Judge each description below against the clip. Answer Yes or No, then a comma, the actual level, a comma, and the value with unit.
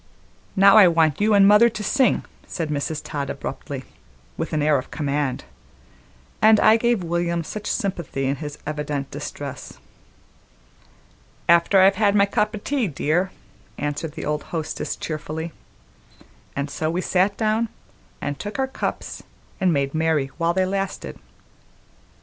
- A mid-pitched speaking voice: Yes, medium, 170 Hz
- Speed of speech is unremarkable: Yes, average, 150 wpm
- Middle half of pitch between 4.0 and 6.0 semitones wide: Yes, average, 5.3 semitones